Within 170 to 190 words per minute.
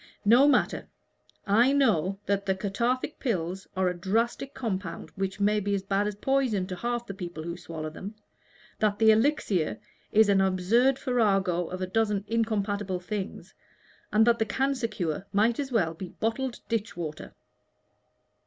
No: average, 160 wpm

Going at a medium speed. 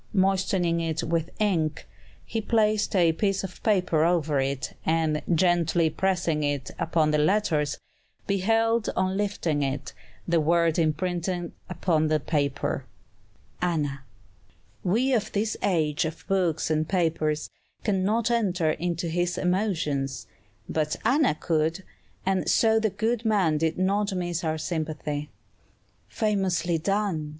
No: slow, 130 wpm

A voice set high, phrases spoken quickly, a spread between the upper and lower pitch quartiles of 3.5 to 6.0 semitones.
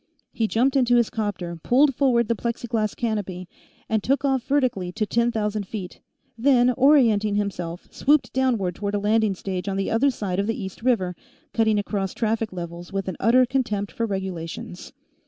No: high, 215 Hz; average, 175 wpm; average, 3.9 semitones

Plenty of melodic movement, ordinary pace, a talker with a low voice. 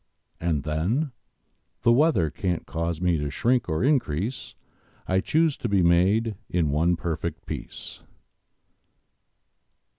No: wide, 6.5 semitones; slow, 120 wpm; very low, 90 Hz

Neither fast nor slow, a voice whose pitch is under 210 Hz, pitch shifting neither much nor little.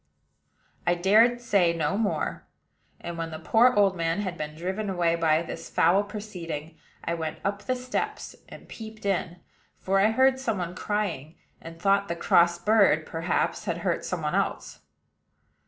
Yes: average, 170 wpm; medium, 185 Hz; average, 3.8 semitones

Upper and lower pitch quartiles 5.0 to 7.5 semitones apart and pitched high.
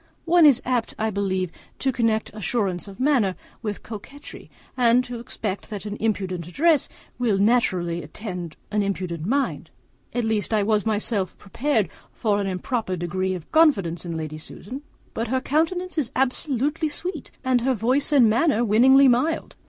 Yes: average, 5.3 semitones; high, 220 Hz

